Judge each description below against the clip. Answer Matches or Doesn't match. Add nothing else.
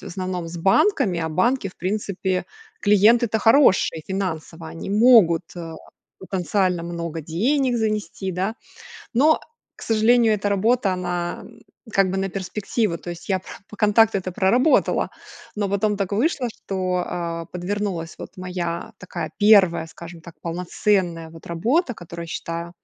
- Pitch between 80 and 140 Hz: Doesn't match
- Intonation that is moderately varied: Matches